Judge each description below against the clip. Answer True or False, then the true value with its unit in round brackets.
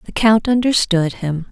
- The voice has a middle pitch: False (200 Hz)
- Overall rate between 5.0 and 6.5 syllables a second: False (4.4 syllables/s)